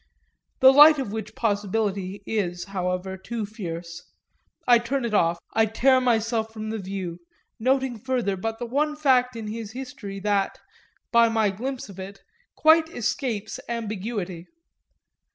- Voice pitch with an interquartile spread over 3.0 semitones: Yes, average, 3.9 semitones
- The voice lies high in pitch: Yes, high, 220 Hz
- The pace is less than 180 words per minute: Yes, average, 145 wpm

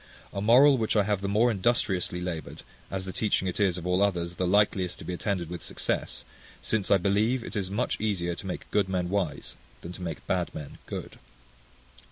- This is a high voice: No, very low, 95 Hz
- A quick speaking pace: Yes, fast, 210 wpm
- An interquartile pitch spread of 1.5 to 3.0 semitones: Yes, average, 2.7 semitones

